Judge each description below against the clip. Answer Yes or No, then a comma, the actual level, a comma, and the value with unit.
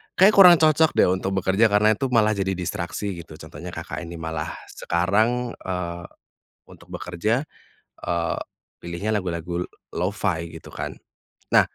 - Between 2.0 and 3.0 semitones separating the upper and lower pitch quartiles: No, average, 4.1 semitones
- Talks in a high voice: No, very low, 95 Hz